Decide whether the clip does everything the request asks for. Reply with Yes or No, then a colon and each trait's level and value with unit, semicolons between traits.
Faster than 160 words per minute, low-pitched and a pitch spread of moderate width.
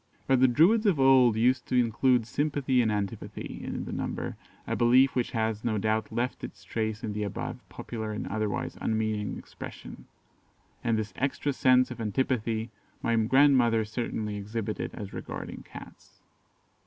No: average, 155 wpm; low, 115 Hz; average, 3.0 semitones